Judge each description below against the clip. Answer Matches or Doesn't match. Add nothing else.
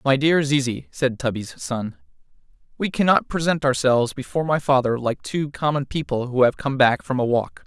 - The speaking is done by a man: Matches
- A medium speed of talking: Matches